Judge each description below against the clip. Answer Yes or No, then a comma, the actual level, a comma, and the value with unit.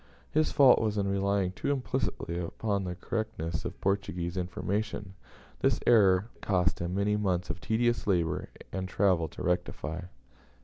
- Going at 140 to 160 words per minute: Yes, average, 150 wpm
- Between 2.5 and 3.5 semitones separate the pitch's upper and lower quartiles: Yes, average, 3.0 semitones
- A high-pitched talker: No, very low, 95 Hz